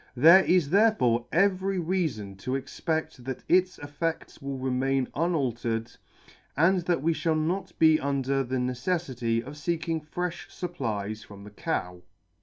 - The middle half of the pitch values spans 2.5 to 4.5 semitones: No, wide, 5.5 semitones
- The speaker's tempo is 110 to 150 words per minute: Yes, average, 140 wpm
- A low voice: No, medium, 145 Hz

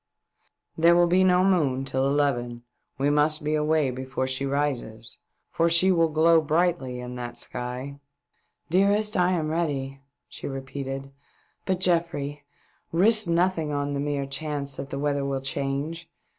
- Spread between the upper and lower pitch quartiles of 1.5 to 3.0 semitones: No, average, 3.7 semitones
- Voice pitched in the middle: Yes, medium, 145 Hz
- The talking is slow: No, average, 160 wpm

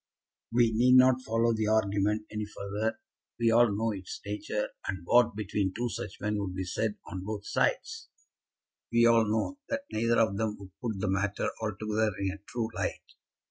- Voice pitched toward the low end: Yes, low, 110 Hz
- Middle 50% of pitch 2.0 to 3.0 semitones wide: Yes, narrow, 2.4 semitones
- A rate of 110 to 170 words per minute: No, average, 180 wpm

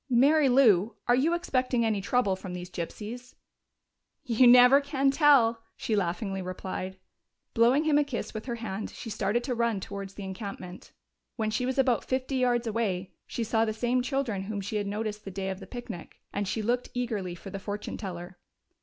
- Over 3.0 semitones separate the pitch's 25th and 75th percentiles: Yes, average, 4.3 semitones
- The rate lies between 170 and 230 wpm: Yes, average, 190 wpm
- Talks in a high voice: Yes, high, 225 Hz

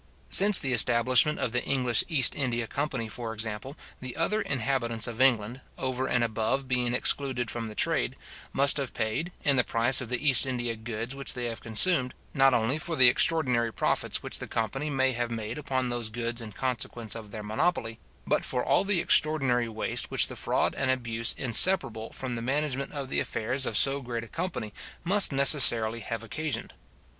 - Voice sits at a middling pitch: No, low, 125 Hz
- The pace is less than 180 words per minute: No, average, 190 wpm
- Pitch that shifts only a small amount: No, average, 3.1 semitones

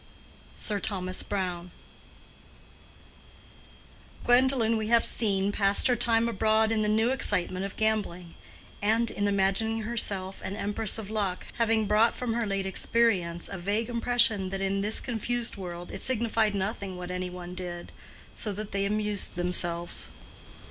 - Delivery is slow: No, average, 150 wpm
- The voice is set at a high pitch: Yes, high, 205 Hz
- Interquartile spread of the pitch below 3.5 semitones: Yes, average, 3.1 semitones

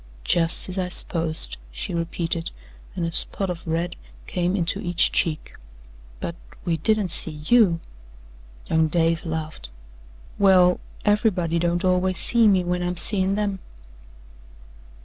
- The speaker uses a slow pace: Yes, slow, 130 wpm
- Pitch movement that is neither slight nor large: No, narrow, 2.2 semitones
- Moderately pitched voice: Yes, medium, 175 Hz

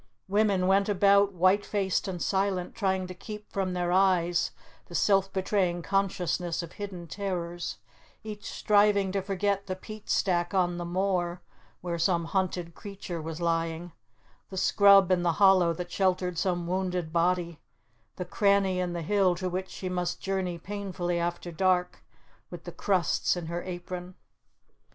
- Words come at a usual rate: Yes, average, 155 wpm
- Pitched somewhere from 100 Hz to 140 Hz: No, medium, 185 Hz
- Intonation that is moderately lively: No, narrow, 2.1 semitones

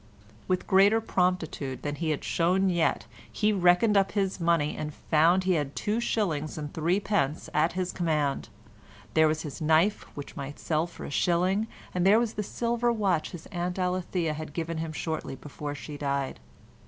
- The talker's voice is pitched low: No, medium, 170 Hz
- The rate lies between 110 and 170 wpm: No, average, 180 wpm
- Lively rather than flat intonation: No, average, 3.8 semitones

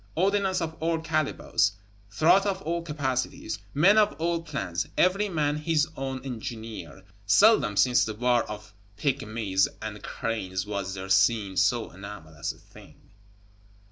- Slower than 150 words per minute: Yes, average, 140 wpm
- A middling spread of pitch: No, wide, 7.9 semitones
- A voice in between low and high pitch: No, low, 125 Hz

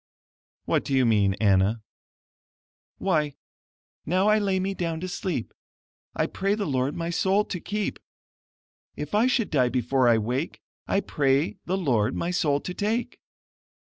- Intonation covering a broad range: Yes, wide, 7.2 semitones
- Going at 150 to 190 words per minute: Yes, average, 155 wpm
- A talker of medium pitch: Yes, medium, 160 Hz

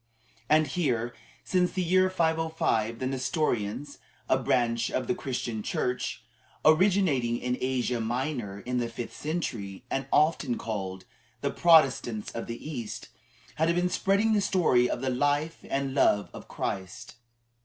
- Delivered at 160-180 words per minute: No, average, 145 wpm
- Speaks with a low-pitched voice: Yes, low, 130 Hz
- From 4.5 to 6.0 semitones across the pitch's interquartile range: Yes, wide, 5.5 semitones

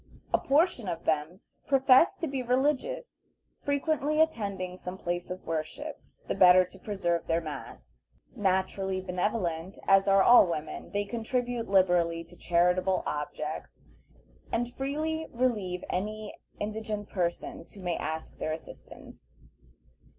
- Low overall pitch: No, high, 190 Hz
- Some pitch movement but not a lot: No, wide, 5.7 semitones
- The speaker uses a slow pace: Yes, slow, 130 wpm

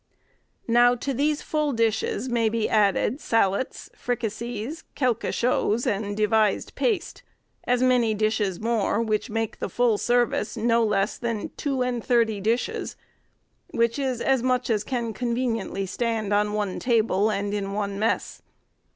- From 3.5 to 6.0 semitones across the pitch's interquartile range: No, narrow, 2.6 semitones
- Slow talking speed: No, average, 145 wpm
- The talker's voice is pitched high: Yes, high, 230 Hz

